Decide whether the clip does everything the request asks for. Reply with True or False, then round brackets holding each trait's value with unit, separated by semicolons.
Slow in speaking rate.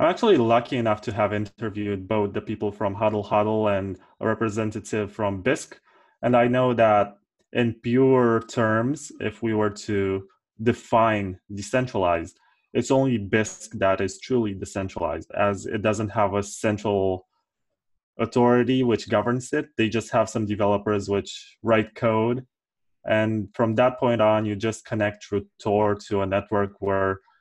False (155 wpm)